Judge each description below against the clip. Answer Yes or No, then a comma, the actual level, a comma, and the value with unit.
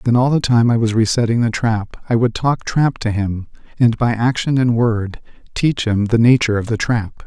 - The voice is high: No, low, 115 Hz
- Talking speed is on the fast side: Yes, fast, 225 wpm